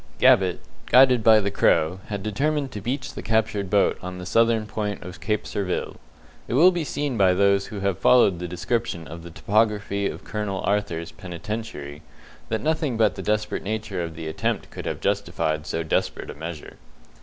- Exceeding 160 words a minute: Yes, average, 185 wpm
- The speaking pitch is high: No, low, 100 Hz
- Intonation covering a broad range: No, average, 3.9 semitones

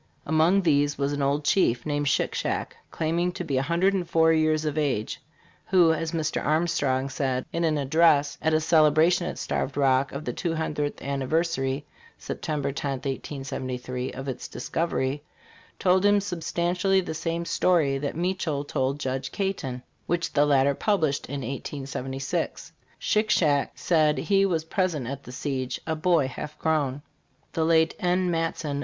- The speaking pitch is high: No, medium, 155 Hz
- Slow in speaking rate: No, average, 165 wpm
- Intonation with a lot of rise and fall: No, average, 3.4 semitones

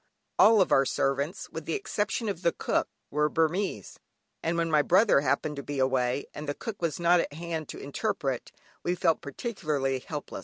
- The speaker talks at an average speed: Yes, average, 185 wpm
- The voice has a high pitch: No, medium, 155 Hz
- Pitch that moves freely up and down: No, average, 4.0 semitones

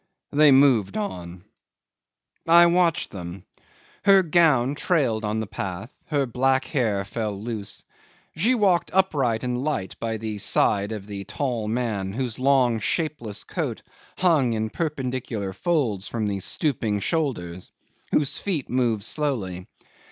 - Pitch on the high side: No, low, 120 Hz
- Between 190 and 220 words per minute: No, slow, 135 wpm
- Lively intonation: Yes, wide, 6.2 semitones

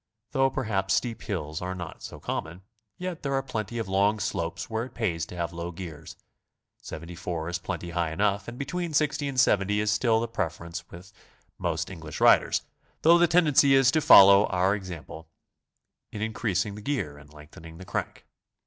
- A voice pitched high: No, low, 100 Hz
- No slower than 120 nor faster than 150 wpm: No, average, 185 wpm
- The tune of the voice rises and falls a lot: Yes, wide, 5.9 semitones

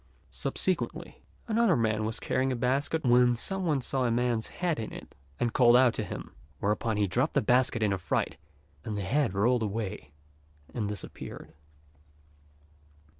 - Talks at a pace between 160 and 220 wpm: Yes, average, 165 wpm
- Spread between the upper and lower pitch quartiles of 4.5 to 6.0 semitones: No, average, 3.3 semitones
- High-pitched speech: No, low, 120 Hz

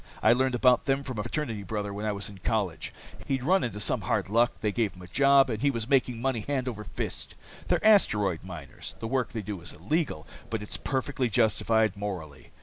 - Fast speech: Yes, fast, 220 wpm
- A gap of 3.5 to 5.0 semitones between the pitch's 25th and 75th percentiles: Yes, average, 4.4 semitones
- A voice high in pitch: No, low, 115 Hz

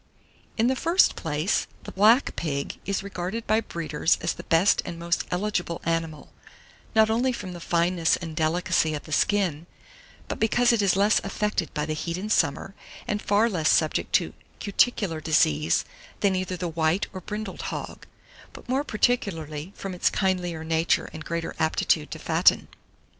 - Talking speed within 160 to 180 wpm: Yes, average, 170 wpm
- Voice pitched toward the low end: No, medium, 180 Hz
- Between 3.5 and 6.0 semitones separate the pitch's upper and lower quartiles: Yes, average, 4.4 semitones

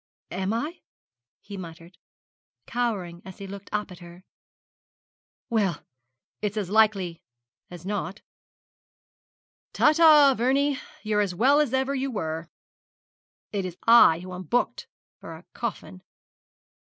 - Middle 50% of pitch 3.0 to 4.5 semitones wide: No, average, 5.2 semitones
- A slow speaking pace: Yes, slow, 125 wpm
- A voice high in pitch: Yes, high, 200 Hz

